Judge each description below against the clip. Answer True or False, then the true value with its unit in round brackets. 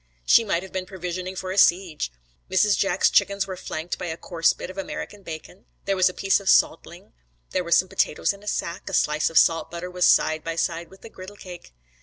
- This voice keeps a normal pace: False (230 wpm)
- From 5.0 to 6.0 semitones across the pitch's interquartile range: False (2.4 semitones)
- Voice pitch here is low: False (185 Hz)